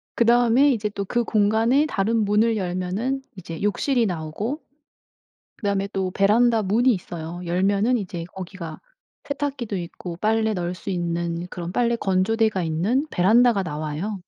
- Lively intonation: No, average, 4.6 semitones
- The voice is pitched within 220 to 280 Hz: No, high, 200 Hz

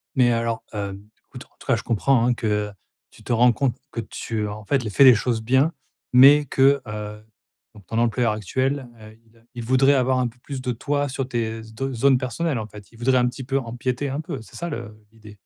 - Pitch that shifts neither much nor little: Yes, average, 3.2 semitones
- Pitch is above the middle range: No, low, 120 Hz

